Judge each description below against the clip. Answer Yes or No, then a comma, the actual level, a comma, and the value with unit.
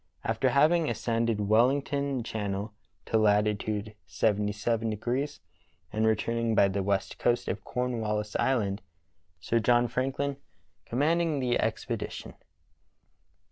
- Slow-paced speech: Yes, slow, 100 wpm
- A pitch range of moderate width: Yes, average, 3.3 semitones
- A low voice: Yes, low, 115 Hz